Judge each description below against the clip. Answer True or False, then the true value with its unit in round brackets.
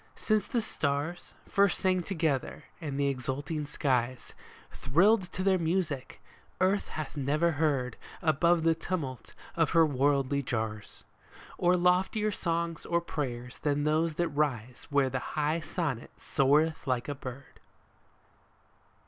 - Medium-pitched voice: True (150 Hz)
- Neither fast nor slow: False (130 wpm)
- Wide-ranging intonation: False (3.9 semitones)